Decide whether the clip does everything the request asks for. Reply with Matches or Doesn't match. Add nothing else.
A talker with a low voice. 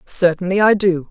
Doesn't match